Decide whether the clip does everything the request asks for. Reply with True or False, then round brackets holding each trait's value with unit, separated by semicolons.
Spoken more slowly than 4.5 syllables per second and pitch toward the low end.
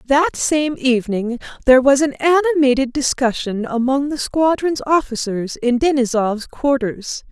False (4.3 syllables/s; 265 Hz)